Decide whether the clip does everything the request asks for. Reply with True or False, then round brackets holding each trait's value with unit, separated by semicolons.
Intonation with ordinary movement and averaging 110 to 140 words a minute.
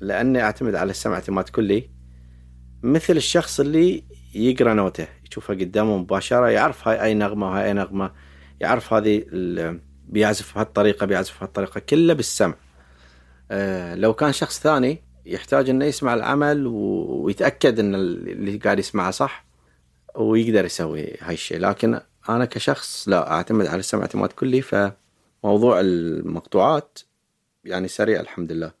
False (5.7 semitones; 130 wpm)